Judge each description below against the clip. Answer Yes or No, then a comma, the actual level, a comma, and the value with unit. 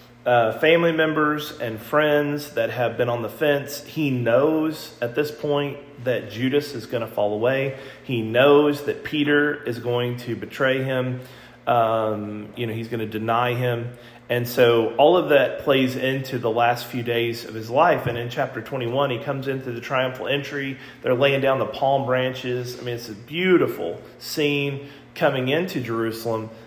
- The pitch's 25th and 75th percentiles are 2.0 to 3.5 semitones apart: Yes, average, 3.1 semitones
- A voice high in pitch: No, low, 130 Hz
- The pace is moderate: Yes, average, 180 wpm